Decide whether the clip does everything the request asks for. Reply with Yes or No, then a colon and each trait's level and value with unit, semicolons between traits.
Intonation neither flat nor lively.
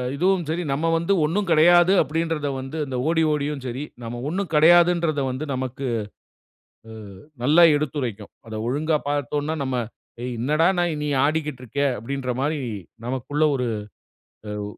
Yes: average, 3.8 semitones